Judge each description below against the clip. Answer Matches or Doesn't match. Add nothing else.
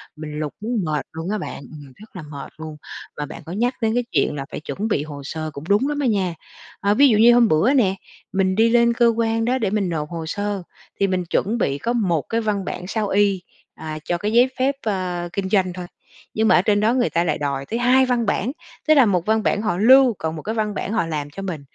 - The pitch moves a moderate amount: Doesn't match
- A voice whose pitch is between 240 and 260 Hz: Doesn't match